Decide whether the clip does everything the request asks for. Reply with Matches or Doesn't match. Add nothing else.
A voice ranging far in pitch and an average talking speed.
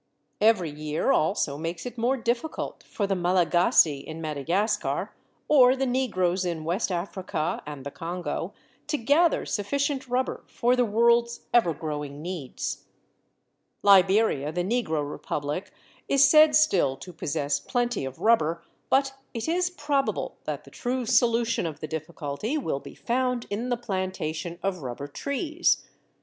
Matches